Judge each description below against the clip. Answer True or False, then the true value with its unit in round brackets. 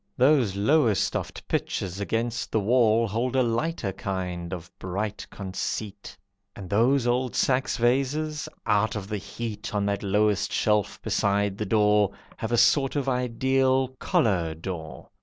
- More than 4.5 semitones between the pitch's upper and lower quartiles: False (4.0 semitones)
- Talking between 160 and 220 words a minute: False (140 wpm)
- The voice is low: True (110 Hz)